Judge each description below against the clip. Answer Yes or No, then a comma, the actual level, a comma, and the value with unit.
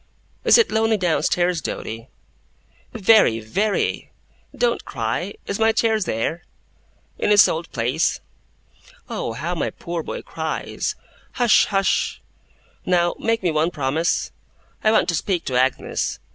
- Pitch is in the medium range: Yes, medium, 175 Hz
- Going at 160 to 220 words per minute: No, slow, 135 wpm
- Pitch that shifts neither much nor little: No, wide, 5.9 semitones